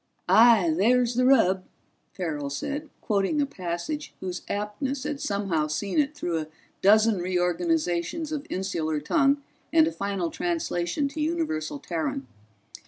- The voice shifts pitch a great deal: Yes, wide, 8.5 semitones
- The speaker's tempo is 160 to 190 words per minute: No, slow, 135 wpm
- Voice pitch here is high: Yes, high, 200 Hz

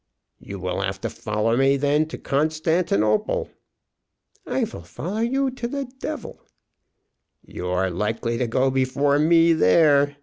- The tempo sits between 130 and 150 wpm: Yes, average, 140 wpm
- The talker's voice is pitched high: No, low, 135 Hz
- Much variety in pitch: Yes, wide, 6.9 semitones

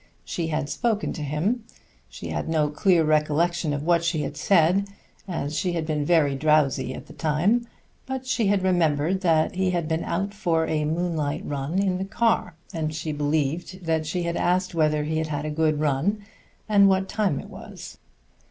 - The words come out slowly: No, average, 190 wpm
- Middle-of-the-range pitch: Yes, medium, 165 Hz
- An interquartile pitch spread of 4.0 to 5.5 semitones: No, average, 3.6 semitones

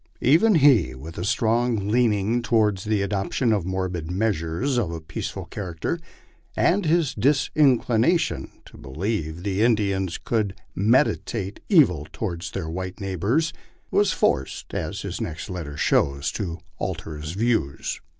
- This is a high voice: No, low, 100 Hz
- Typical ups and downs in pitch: No, wide, 5.9 semitones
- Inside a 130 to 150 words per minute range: Yes, average, 140 wpm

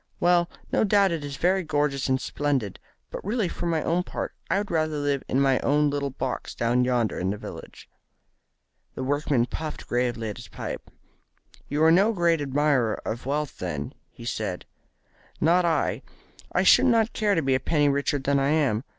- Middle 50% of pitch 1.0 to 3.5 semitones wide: No, average, 4.4 semitones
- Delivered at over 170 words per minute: Yes, average, 190 wpm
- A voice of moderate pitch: Yes, medium, 145 Hz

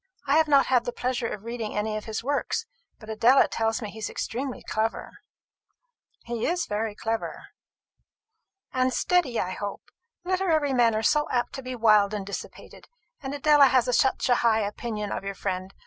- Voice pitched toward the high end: Yes, high, 235 Hz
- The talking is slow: No, average, 180 wpm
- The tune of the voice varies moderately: Yes, average, 3.8 semitones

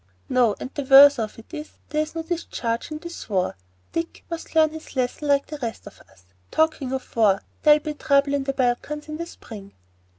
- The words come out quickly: Yes, fast, 210 wpm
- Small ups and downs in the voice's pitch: No, average, 4.2 semitones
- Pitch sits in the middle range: No, very high, 280 Hz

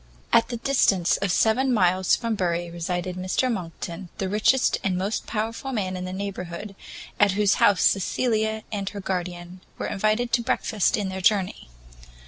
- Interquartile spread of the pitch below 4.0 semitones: Yes, average, 3.2 semitones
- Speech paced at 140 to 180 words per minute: Yes, average, 165 wpm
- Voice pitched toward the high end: Yes, high, 195 Hz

